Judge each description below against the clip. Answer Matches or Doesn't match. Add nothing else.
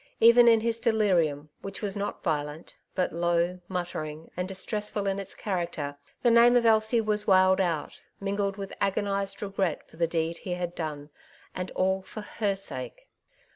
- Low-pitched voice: Doesn't match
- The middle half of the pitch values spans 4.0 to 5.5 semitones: Doesn't match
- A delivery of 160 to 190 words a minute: Matches